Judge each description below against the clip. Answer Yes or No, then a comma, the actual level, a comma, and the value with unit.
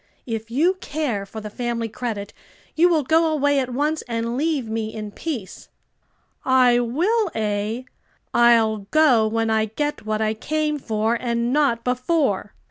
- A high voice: Yes, high, 240 Hz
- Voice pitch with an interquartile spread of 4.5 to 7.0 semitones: Yes, average, 5.2 semitones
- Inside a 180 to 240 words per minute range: No, average, 155 wpm